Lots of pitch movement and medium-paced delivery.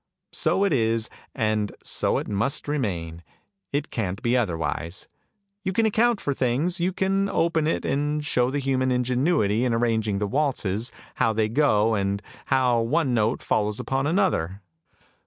Yes: wide, 5.7 semitones; average, 155 wpm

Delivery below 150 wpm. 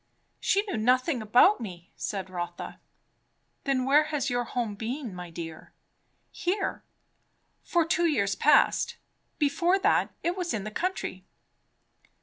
Yes: slow, 135 wpm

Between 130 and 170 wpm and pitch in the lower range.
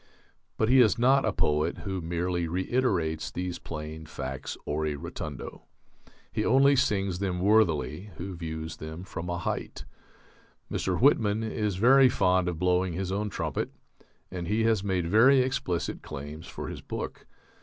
Yes: average, 155 wpm; very low, 90 Hz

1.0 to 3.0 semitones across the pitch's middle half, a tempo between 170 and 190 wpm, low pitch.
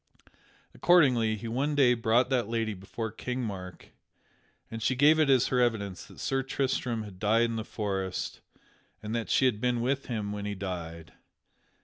No: average, 3.6 semitones; average, 175 wpm; low, 115 Hz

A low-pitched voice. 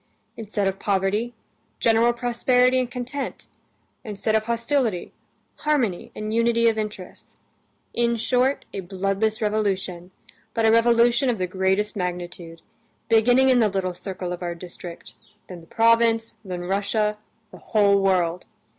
No: high, 215 Hz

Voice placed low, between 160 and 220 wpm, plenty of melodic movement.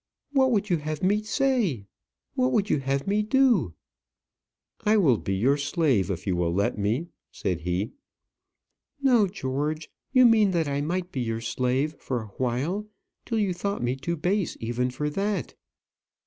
No: medium, 150 Hz; average, 165 wpm; wide, 8.7 semitones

